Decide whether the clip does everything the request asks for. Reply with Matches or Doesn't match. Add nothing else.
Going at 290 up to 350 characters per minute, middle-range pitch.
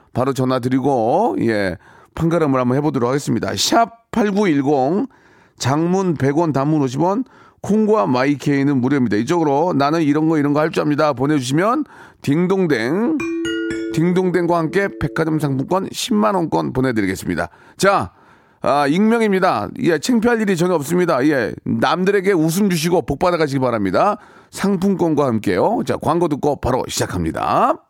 Matches